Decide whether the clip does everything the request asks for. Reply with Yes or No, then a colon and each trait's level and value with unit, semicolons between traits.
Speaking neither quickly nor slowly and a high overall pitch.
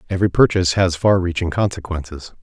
No: average, 150 wpm; very low, 90 Hz